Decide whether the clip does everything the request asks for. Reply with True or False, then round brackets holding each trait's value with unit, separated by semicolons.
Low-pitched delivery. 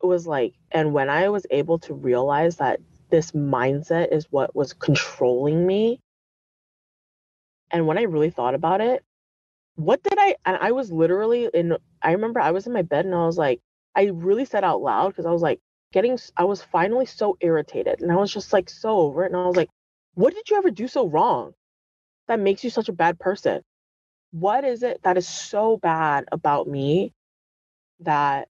False (175 Hz)